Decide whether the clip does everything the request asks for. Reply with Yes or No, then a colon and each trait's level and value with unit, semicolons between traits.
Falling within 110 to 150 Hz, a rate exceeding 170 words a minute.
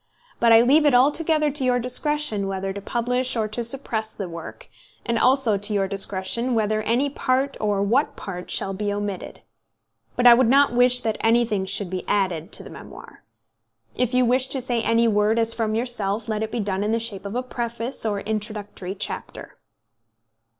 No: high, 225 Hz; average, 190 wpm